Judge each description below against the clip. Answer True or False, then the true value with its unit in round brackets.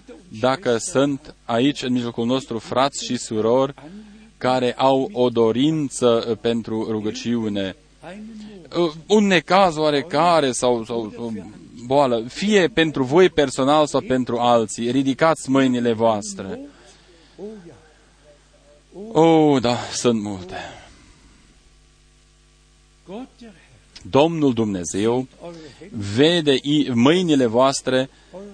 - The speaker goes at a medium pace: False (85 wpm)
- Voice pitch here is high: False (135 Hz)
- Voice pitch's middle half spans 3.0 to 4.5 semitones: False (5.3 semitones)